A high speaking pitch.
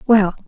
Yes: high, 205 Hz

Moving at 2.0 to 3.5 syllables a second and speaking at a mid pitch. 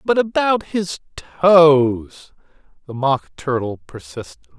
Yes: 3.3 syllables/s; medium, 150 Hz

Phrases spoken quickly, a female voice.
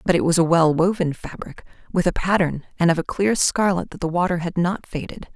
Yes: fast, 235 wpm; female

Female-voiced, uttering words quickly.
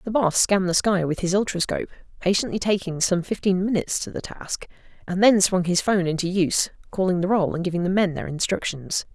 Yes: female; fast, 210 wpm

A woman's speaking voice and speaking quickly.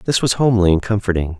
No: male; fast, 215 wpm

